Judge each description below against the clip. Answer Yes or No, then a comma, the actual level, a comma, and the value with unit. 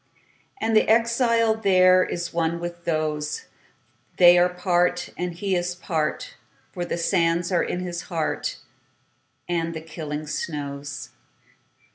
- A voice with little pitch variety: Yes, narrow, 1.9 semitones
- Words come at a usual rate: No, slow, 110 wpm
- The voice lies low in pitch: No, medium, 175 Hz